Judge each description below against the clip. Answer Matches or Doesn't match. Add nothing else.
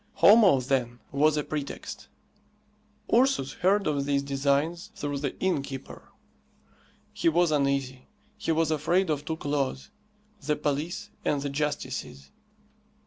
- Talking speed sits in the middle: Doesn't match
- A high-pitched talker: Doesn't match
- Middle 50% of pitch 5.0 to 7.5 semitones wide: Doesn't match